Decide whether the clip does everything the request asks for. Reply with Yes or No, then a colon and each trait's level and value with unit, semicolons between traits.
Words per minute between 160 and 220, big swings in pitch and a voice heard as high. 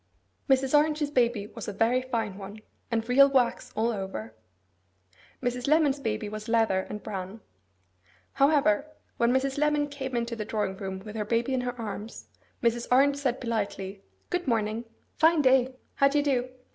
No: average, 170 wpm; average, 4.1 semitones; high, 240 Hz